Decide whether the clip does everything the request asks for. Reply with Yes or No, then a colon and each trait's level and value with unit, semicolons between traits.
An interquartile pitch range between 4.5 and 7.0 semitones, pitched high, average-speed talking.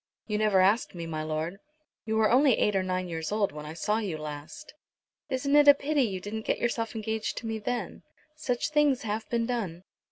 No: average, 4.8 semitones; high, 215 Hz; fast, 215 wpm